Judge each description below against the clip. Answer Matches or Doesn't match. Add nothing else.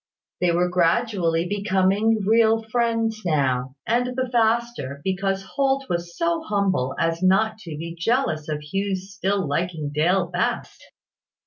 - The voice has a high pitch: Matches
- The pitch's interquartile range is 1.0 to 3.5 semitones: Doesn't match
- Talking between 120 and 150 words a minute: Matches